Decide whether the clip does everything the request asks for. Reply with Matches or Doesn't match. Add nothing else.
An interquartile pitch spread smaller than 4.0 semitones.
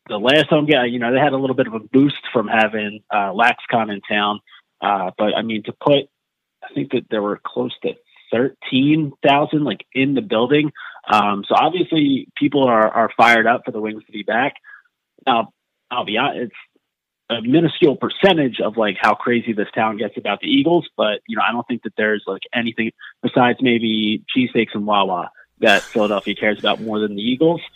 Doesn't match